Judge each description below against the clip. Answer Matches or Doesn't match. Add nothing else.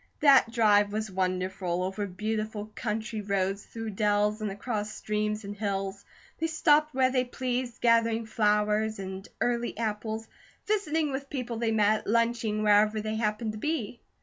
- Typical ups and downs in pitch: Doesn't match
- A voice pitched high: Matches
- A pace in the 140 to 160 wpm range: Matches